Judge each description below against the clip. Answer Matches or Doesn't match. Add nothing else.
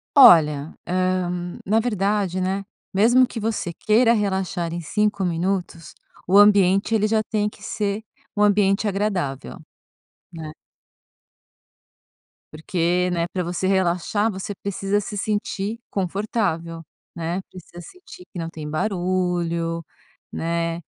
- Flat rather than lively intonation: Doesn't match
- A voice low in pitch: Doesn't match